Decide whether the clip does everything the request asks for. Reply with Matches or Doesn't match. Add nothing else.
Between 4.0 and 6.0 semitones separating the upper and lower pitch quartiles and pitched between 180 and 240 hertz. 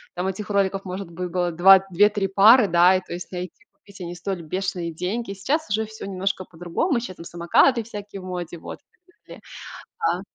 Doesn't match